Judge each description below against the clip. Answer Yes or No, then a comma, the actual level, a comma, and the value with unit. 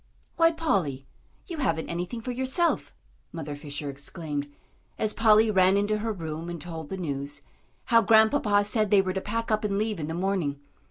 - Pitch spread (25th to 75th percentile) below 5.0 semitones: No, wide, 5.5 semitones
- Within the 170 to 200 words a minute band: Yes, average, 180 wpm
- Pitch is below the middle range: No, high, 195 Hz